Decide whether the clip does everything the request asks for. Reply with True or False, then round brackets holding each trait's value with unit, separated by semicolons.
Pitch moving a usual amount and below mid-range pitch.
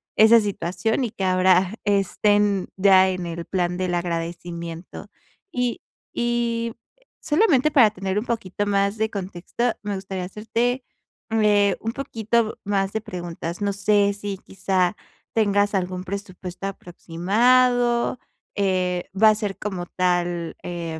False (3.3 semitones; 200 Hz)